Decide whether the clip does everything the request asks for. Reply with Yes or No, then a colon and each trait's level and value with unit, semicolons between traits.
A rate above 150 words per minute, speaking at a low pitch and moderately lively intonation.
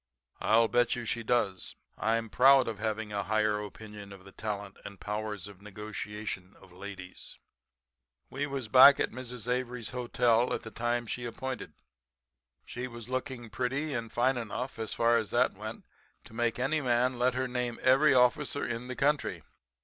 Yes: average, 175 wpm; low, 120 Hz; average, 3.0 semitones